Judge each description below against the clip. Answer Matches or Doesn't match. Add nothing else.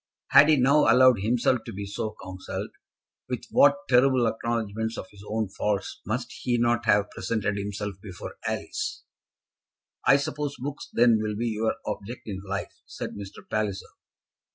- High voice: Doesn't match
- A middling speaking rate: Matches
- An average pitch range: Matches